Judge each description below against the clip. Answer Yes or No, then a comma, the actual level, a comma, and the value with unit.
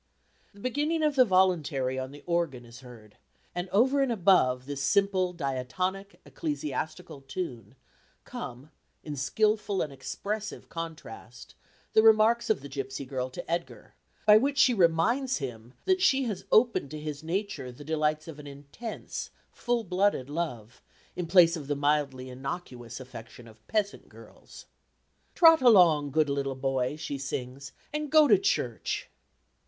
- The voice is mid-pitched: Yes, medium, 160 Hz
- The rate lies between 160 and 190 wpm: No, average, 150 wpm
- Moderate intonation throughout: No, wide, 7.7 semitones